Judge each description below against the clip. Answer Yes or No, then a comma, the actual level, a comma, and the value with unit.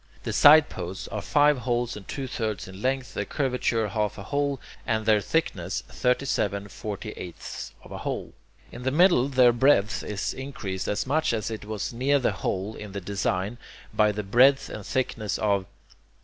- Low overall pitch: Yes, low, 110 Hz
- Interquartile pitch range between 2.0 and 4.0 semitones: No, average, 4.5 semitones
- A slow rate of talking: No, average, 180 wpm